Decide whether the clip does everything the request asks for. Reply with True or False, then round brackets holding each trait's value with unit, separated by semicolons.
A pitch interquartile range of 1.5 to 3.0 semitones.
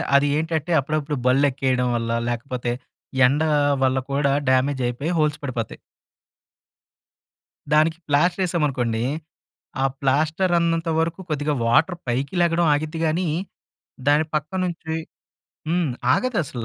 False (3.8 semitones)